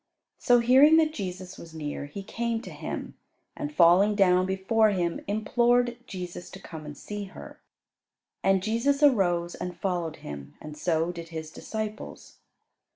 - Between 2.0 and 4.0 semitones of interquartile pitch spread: No, average, 5.0 semitones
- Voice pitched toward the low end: No, high, 190 Hz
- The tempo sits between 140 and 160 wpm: Yes, average, 155 wpm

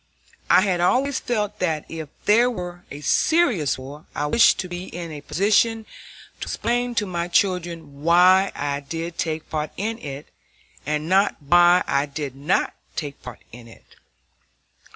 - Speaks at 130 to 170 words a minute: Yes, average, 160 wpm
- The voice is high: No, medium, 175 Hz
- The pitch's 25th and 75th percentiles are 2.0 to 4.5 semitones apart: No, average, 5.0 semitones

